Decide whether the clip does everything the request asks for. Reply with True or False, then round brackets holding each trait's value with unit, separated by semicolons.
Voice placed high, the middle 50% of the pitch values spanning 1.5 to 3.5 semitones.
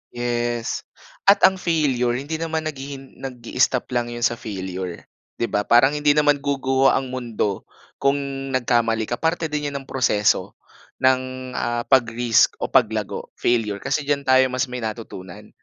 False (130 Hz; 3.0 semitones)